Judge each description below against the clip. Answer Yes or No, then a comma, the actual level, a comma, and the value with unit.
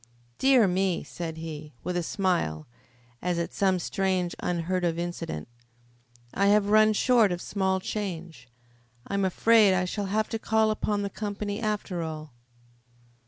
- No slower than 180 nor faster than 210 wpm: No, average, 155 wpm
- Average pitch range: Yes, average, 3.3 semitones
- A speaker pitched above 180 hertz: Yes, high, 190 Hz